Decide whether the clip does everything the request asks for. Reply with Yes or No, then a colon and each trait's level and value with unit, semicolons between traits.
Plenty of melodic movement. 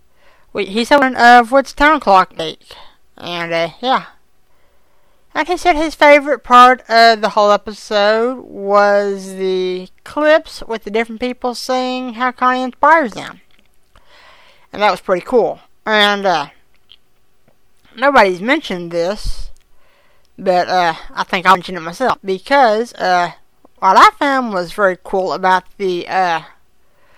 Yes: wide, 6.5 semitones